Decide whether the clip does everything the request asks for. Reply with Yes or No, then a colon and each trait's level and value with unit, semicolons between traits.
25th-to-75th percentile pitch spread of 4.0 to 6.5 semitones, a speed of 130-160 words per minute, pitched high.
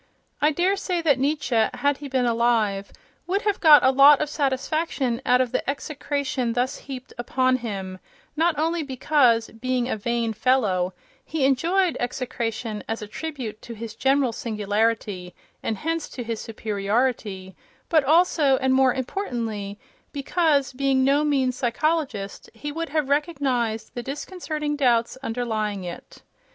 Yes: average, 4.4 semitones; average, 145 wpm; very high, 260 Hz